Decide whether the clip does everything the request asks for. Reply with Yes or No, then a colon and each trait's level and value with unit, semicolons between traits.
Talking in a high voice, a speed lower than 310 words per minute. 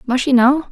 Yes: very high, 260 Hz; fast, 250 wpm